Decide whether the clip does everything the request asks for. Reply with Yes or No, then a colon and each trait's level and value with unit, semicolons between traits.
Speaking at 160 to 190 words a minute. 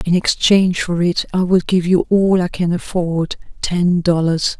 Yes: average, 170 wpm